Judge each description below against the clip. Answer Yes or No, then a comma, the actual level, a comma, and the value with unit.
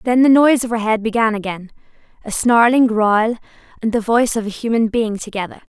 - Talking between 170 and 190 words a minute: Yes, average, 180 wpm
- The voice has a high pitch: Yes, high, 225 Hz